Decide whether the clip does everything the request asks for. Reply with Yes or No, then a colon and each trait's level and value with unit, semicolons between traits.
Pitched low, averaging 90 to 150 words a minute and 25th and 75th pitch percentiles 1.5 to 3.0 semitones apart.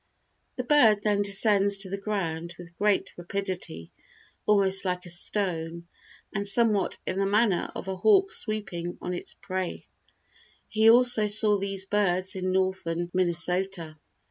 No: high, 195 Hz; average, 145 wpm; average, 2.7 semitones